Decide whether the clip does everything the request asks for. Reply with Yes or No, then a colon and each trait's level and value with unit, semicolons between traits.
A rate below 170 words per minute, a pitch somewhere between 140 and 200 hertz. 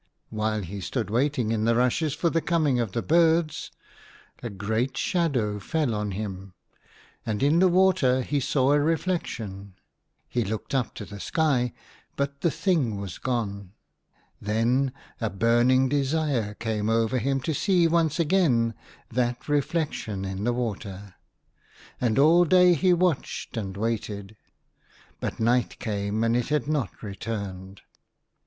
No: average, 150 wpm; low, 120 Hz